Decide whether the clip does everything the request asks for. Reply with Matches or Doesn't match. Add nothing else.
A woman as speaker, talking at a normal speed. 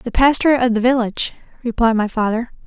Matches